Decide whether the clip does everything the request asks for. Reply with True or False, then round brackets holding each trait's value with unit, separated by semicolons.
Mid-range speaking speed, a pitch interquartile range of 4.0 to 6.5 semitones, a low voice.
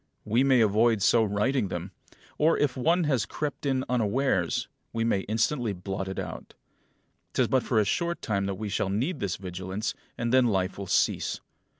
True (185 wpm; 4.8 semitones; 110 Hz)